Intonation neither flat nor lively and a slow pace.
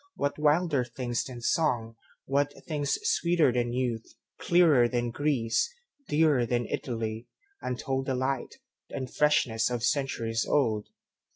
Yes: average, 3.8 semitones; slow, 100 wpm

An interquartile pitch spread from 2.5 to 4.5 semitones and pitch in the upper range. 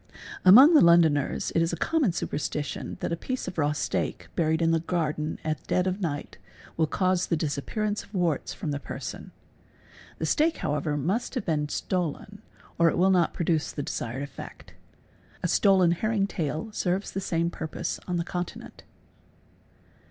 No: average, 3.6 semitones; medium, 170 Hz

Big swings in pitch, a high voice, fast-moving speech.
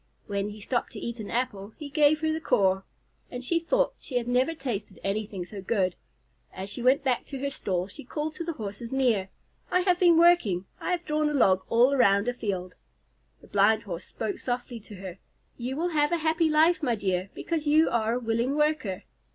Yes: wide, 7.1 semitones; high, 245 Hz; fast, 215 wpm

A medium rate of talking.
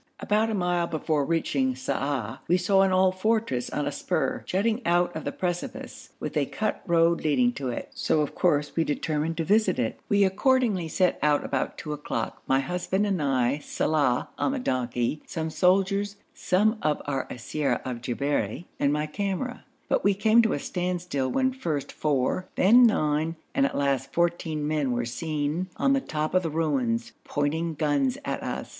Yes: average, 185 wpm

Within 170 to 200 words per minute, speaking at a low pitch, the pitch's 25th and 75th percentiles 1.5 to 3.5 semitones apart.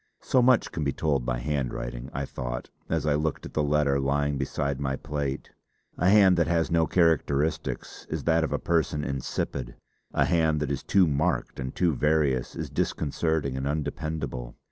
Yes: average, 180 wpm; very low, 75 Hz; average, 2.9 semitones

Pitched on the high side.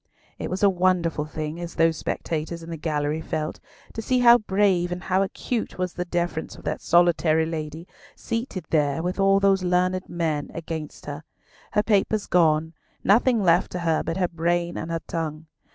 No: medium, 175 Hz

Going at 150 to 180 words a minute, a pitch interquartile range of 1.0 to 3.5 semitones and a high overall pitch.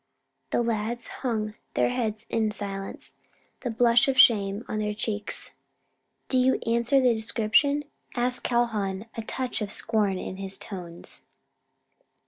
No: slow, 135 wpm; narrow, 2.6 semitones; high, 225 Hz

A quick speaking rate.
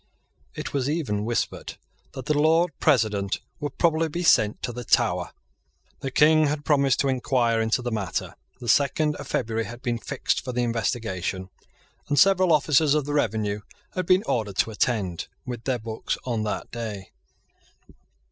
No: average, 165 wpm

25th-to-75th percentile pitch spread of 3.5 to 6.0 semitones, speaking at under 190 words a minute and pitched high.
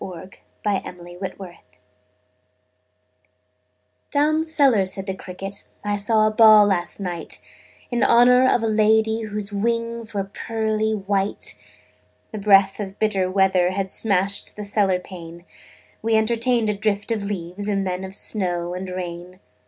No: average, 2.7 semitones; average, 140 wpm; high, 200 Hz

